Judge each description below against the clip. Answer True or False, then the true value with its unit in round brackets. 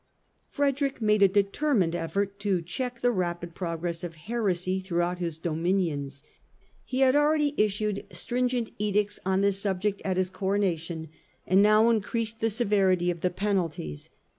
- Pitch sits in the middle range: False (195 Hz)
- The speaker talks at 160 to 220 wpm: True (165 wpm)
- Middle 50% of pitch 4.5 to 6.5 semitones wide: False (3.9 semitones)